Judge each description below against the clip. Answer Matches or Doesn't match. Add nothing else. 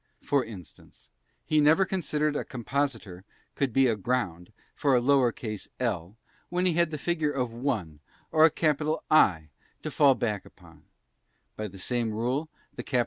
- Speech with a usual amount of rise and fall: Doesn't match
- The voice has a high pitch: Doesn't match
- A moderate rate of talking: Matches